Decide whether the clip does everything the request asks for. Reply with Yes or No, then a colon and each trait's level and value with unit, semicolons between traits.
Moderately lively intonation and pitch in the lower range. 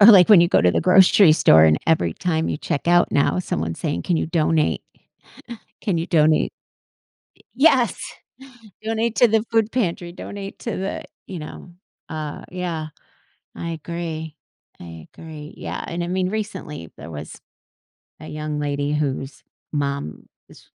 No: average, 4.1 semitones; medium, 165 Hz